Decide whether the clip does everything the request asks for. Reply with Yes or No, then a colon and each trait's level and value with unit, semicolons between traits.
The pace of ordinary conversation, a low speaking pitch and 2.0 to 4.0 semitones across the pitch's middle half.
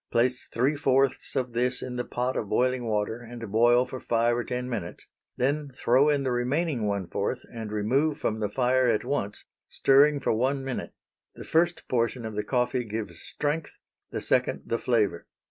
Yes: average, 185 wpm; low, 125 Hz; average, 2.9 semitones